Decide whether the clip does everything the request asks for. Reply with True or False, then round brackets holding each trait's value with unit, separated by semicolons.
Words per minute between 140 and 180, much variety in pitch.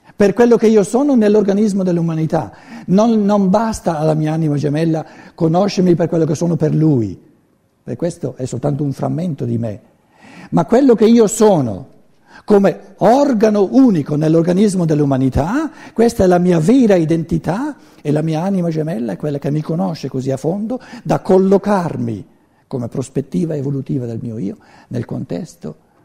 True (155 wpm; 6.0 semitones)